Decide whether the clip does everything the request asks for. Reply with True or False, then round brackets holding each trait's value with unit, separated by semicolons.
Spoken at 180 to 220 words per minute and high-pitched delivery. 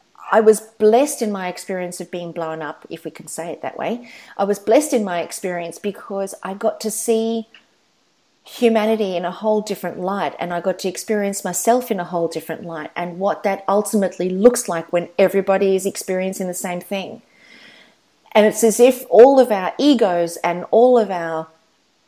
True (190 wpm; 195 Hz)